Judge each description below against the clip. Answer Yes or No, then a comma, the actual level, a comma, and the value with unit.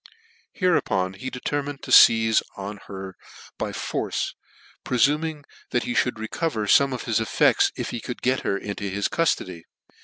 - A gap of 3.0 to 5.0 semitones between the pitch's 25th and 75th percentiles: No, wide, 5.6 semitones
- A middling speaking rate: Yes, average, 155 wpm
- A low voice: Yes, low, 115 Hz